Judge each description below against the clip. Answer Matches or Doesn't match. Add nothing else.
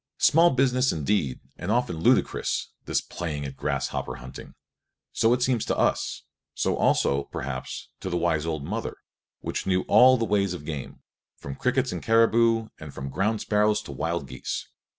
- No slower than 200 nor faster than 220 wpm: Doesn't match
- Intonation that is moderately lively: Doesn't match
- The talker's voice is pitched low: Matches